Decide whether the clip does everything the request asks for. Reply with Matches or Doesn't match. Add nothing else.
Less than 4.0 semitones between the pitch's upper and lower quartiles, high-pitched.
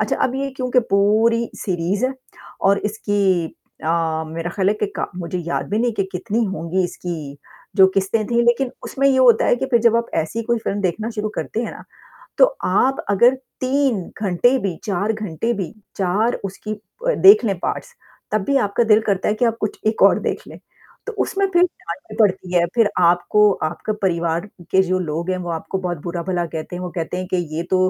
Doesn't match